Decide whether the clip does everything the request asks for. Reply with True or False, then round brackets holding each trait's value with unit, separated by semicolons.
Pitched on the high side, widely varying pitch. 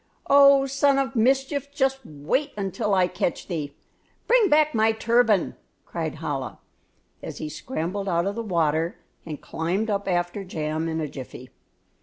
True (200 Hz; 8.4 semitones)